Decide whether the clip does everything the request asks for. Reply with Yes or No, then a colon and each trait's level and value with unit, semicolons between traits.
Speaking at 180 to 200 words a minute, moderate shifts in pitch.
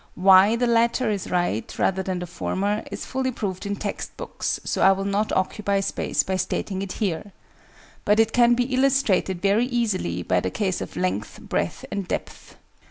Yes: average, 185 wpm; average, 3.6 semitones